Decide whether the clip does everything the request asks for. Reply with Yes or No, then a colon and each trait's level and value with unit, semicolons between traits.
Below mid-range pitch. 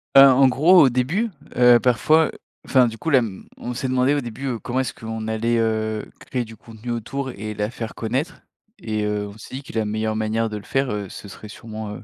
Yes: low, 115 Hz